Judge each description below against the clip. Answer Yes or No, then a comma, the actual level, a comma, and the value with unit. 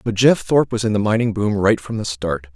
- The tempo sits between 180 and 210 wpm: No, fast, 280 wpm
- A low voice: Yes, low, 110 Hz